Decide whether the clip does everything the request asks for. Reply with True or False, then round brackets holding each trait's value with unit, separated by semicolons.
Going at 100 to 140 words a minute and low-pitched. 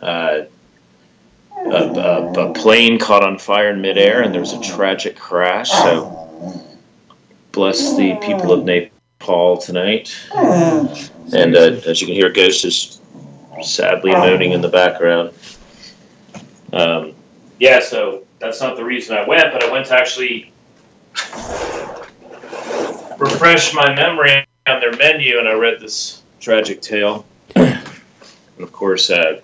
True (135 wpm; 120 Hz)